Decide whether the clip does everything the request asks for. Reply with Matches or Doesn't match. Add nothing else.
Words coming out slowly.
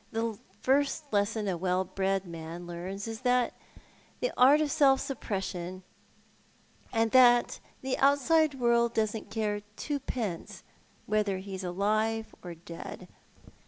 Matches